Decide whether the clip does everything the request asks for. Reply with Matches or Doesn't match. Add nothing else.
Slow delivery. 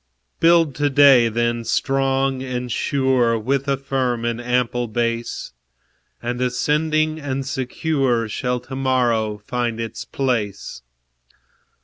Matches